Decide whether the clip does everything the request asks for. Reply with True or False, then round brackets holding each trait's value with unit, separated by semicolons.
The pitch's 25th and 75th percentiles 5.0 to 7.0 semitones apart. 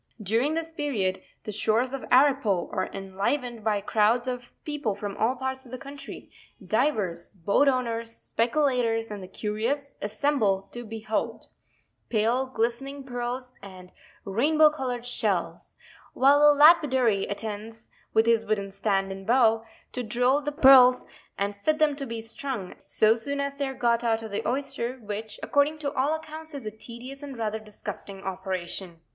False (4.5 semitones)